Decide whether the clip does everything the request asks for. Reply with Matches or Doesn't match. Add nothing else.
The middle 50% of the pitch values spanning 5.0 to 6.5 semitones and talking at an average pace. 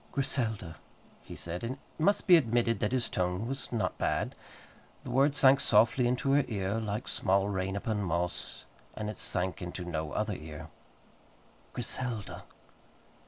Matches